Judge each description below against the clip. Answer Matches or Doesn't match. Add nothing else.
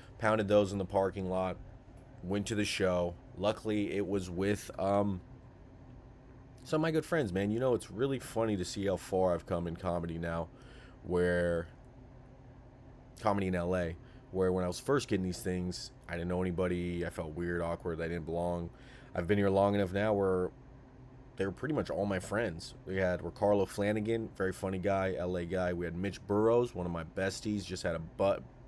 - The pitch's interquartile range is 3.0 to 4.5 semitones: Doesn't match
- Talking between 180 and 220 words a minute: Matches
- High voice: Doesn't match